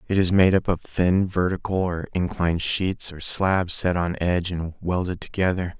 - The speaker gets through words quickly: No, average, 185 wpm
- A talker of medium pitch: No, very low, 90 Hz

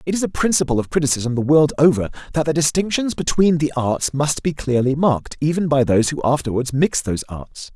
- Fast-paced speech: Yes, fast, 210 wpm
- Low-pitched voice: No, medium, 145 Hz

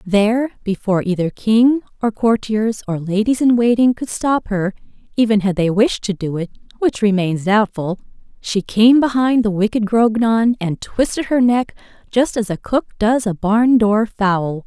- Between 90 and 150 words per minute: No, average, 165 wpm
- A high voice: Yes, high, 215 Hz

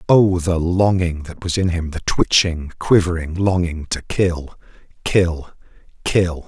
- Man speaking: Yes, male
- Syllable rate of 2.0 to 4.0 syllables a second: Yes, 3.8 syllables/s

